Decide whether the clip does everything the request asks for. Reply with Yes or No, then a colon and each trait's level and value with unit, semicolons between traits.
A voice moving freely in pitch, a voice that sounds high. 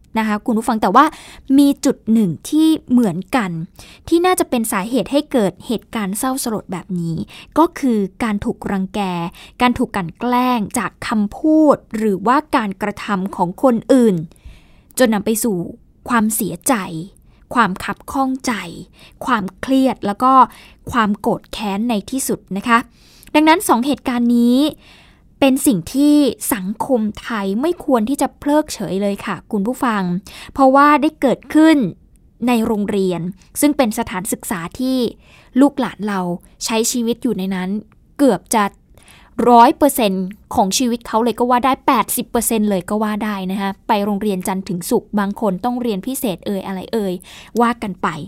No: average, 4.6 semitones; high, 230 Hz